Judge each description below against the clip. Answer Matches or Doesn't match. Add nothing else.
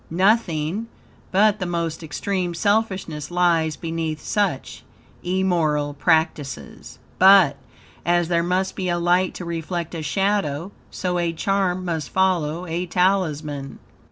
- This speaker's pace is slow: Matches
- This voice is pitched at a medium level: Matches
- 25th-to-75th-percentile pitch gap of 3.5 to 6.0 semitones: Doesn't match